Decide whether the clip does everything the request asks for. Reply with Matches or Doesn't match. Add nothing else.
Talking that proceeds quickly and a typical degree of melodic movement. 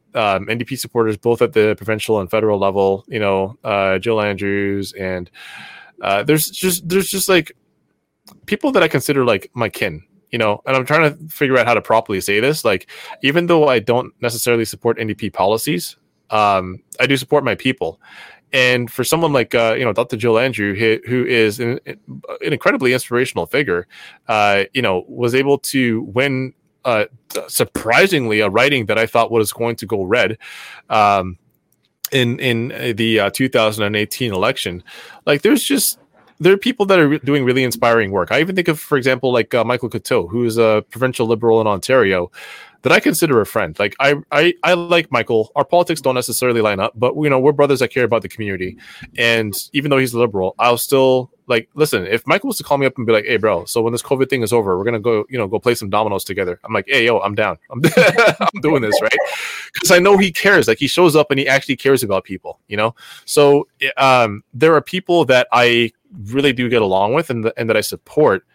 Matches